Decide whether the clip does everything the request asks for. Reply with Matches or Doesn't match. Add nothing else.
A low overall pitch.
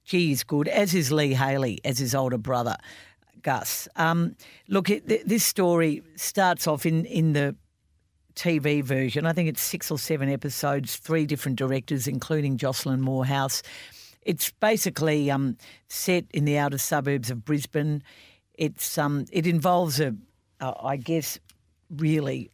Doesn't match